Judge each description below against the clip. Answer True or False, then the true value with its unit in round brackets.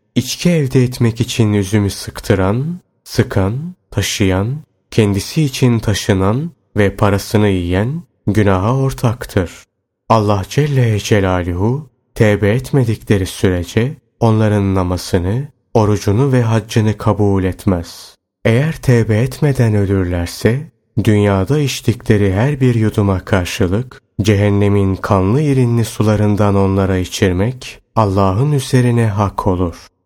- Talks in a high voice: False (105 Hz)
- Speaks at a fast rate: False (100 wpm)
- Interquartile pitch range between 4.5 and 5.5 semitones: False (4.0 semitones)